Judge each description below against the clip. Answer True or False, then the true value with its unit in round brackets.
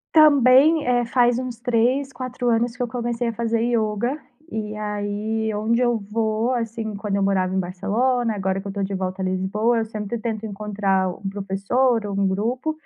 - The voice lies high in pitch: True (220 Hz)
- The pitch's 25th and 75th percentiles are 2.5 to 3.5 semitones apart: True (3.2 semitones)